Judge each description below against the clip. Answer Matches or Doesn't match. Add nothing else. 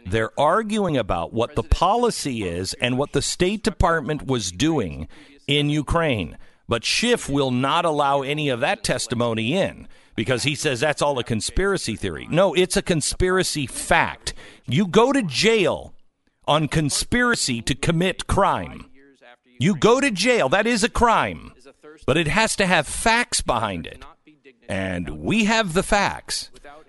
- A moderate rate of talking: Matches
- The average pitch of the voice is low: Doesn't match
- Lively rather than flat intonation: Matches